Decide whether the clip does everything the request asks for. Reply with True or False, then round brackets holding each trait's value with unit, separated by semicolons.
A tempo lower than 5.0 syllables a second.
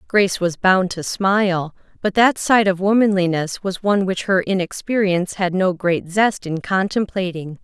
True (4.7 syllables/s)